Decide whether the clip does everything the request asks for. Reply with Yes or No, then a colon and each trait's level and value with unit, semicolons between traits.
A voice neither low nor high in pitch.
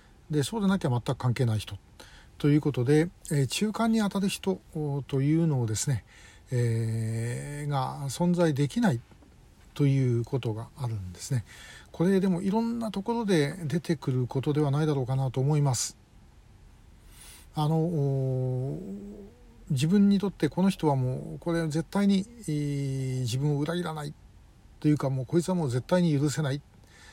Yes: medium, 145 Hz